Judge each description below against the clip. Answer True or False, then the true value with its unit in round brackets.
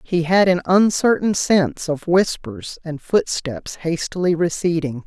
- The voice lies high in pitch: False (170 Hz)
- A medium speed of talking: False (130 wpm)